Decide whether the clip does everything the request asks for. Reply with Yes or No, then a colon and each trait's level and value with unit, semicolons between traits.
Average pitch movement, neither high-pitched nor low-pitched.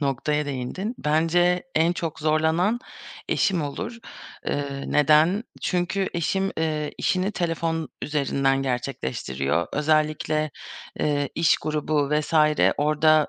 Yes: average, 3.1 semitones; medium, 155 Hz